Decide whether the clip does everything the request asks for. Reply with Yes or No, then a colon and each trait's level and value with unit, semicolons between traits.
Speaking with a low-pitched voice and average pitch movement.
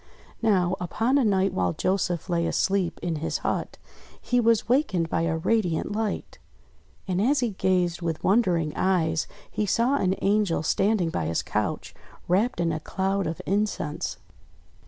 No: high, 190 Hz; average, 4.2 semitones